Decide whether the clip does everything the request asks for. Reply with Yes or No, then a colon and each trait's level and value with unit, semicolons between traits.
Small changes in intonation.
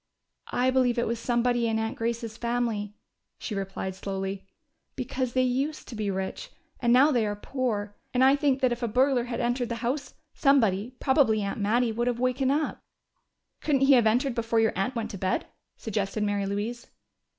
No: average, 3.3 semitones